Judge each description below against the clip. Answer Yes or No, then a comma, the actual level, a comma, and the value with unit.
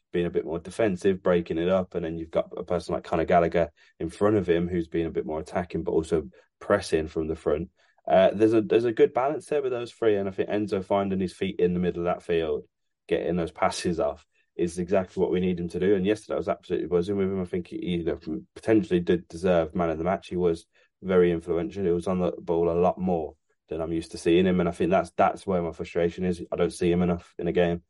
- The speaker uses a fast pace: Yes, fast, 265 wpm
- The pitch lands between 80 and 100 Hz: Yes, very low, 90 Hz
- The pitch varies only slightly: No, average, 3.1 semitones